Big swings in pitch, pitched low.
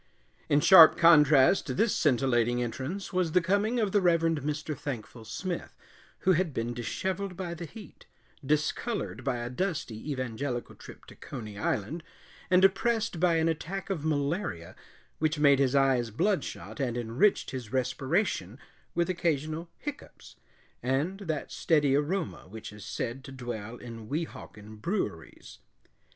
No: wide, 6.6 semitones; medium, 145 Hz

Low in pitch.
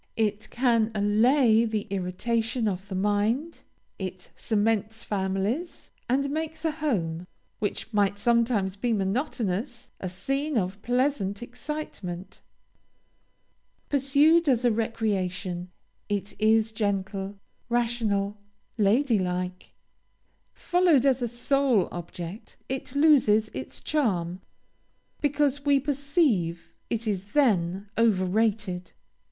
No: high, 220 Hz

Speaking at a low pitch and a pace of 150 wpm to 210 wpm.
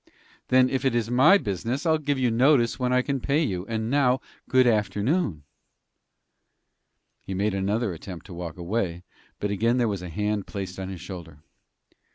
Yes: low, 110 Hz; average, 180 wpm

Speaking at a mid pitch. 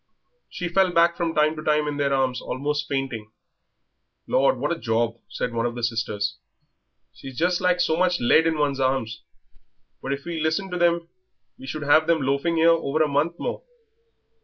Yes: medium, 150 Hz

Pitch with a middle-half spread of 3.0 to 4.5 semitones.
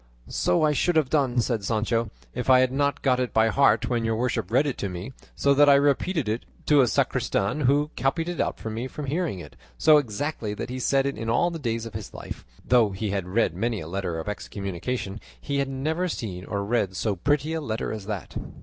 No: average, 4.9 semitones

